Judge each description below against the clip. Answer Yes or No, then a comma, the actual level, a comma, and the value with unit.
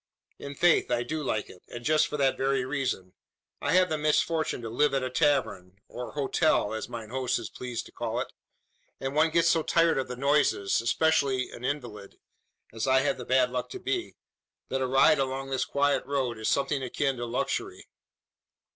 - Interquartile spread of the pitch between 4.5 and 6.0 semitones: No, average, 3.2 semitones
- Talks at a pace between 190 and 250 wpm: Yes, average, 200 wpm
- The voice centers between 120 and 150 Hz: Yes, low, 135 Hz